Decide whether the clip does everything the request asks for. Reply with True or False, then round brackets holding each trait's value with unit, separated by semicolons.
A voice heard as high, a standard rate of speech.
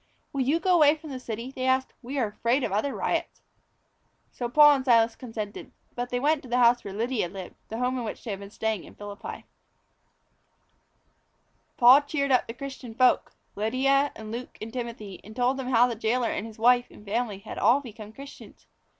False (245 Hz; 210 wpm)